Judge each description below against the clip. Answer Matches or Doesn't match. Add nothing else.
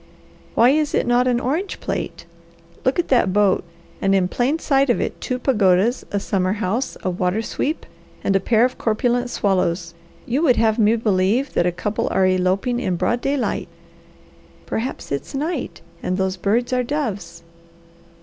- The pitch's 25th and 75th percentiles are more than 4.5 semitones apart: Matches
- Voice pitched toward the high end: Matches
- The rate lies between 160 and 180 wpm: Matches